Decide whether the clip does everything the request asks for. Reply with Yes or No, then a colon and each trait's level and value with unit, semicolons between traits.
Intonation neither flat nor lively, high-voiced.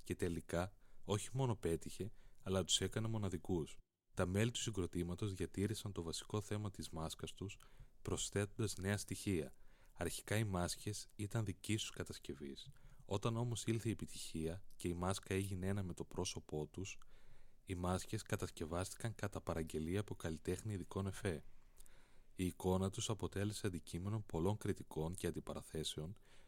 No: average, 3.6 semitones; very low, 95 Hz